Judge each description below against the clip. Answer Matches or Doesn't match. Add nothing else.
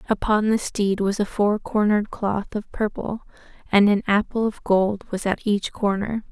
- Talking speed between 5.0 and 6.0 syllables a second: Doesn't match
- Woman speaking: Matches